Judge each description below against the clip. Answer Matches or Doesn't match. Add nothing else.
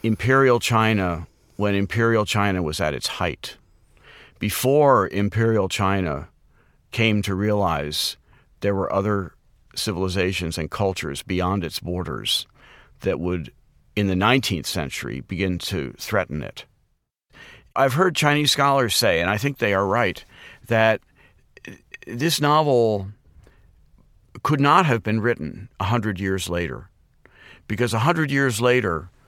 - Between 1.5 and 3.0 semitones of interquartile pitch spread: Doesn't match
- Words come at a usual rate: Doesn't match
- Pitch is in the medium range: Doesn't match